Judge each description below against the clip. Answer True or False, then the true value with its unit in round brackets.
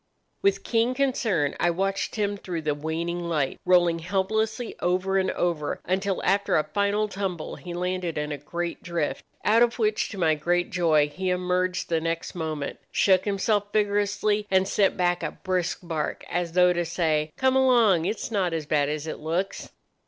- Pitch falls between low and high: True (180 Hz)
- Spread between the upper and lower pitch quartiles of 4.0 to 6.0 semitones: False (3.4 semitones)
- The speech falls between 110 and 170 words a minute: False (180 wpm)